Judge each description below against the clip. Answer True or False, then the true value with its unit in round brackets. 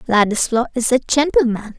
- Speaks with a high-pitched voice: True (240 Hz)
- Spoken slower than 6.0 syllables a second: True (5.7 syllables/s)